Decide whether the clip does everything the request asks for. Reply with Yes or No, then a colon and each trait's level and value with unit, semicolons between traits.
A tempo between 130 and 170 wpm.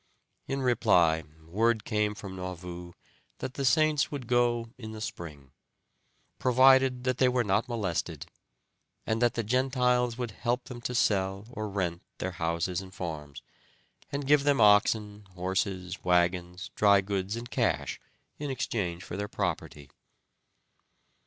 Yes: average, 140 wpm